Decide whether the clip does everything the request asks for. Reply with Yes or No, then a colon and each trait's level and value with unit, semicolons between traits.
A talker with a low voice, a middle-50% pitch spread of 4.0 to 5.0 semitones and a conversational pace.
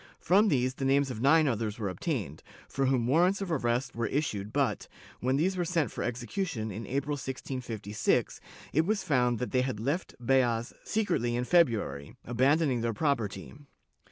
Yes: low, 130 Hz; average, 4.7 semitones; average, 170 wpm